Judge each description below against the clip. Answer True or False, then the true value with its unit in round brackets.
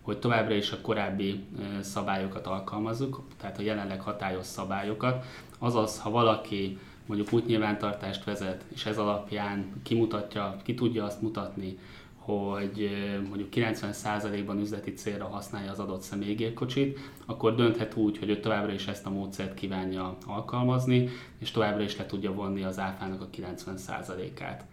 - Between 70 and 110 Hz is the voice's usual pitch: True (105 Hz)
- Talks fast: False (140 wpm)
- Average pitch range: False (2.1 semitones)